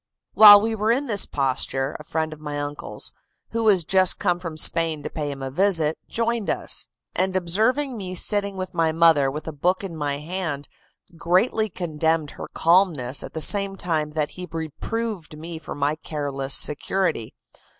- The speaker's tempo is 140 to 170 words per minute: No, average, 180 wpm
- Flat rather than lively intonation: No, average, 4.4 semitones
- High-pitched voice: No, medium, 165 Hz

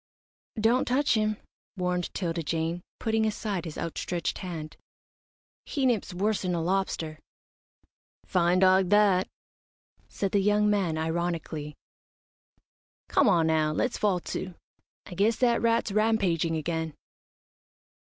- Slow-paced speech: Yes, slow, 120 wpm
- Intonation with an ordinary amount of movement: Yes, average, 4.2 semitones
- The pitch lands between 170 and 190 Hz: Yes, medium, 185 Hz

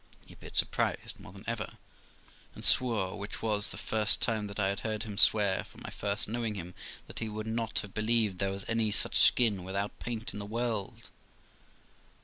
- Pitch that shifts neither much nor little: No, narrow, 2.1 semitones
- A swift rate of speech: No, average, 195 wpm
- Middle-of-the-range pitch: No, low, 105 Hz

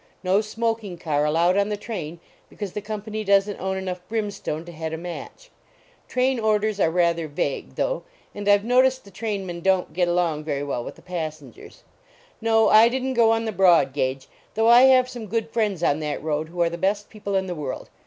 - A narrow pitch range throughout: No, average, 4.7 semitones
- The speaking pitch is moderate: No, high, 195 Hz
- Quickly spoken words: Yes, fast, 220 wpm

